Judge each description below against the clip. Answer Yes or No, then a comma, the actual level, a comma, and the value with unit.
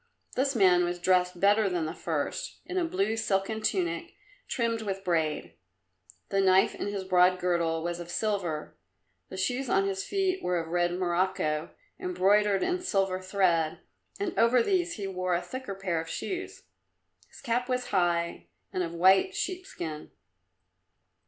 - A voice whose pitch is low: No, high, 190 Hz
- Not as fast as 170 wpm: Yes, average, 160 wpm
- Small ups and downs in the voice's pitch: No, average, 4.7 semitones